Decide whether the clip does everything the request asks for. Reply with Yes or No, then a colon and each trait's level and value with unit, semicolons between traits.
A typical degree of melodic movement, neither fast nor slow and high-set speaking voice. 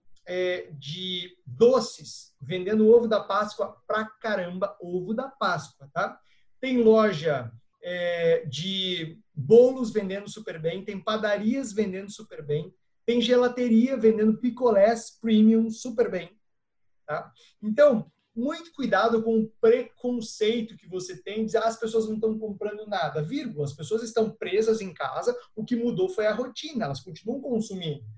Yes: average, 4.3 semitones; average, 145 wpm; high, 215 Hz